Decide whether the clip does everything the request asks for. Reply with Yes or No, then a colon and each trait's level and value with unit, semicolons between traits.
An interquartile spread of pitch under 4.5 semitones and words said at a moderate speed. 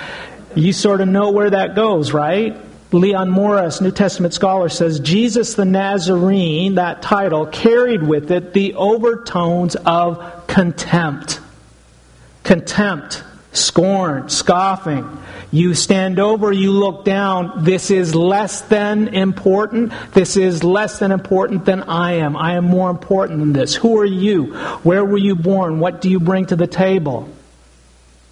Yes: average, 2.9 semitones; average, 145 wpm